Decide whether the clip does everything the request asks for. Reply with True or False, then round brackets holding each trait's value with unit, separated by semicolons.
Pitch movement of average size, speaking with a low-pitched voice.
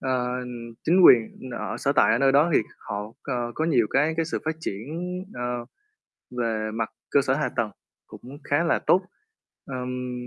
True (3.3 semitones; 125 Hz)